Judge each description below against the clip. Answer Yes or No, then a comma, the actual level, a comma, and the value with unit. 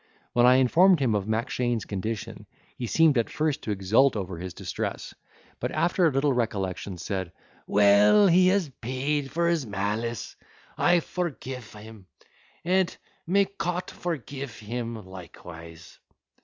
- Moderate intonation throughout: No, wide, 7.7 semitones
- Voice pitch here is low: Yes, low, 120 Hz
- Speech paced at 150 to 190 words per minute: No, average, 140 wpm